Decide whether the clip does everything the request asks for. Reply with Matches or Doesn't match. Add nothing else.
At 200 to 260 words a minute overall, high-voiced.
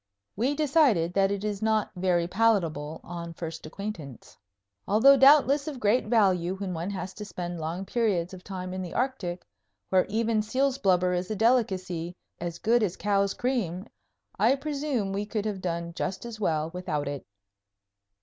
Doesn't match